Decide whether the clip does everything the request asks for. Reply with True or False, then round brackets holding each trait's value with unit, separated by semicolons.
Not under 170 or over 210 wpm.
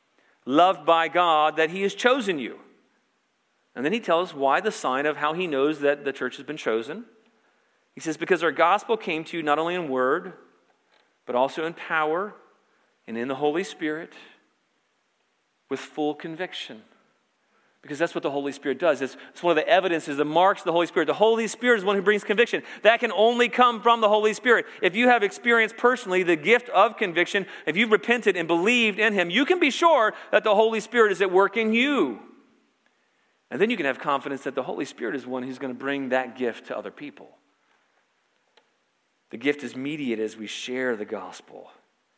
True (205 wpm)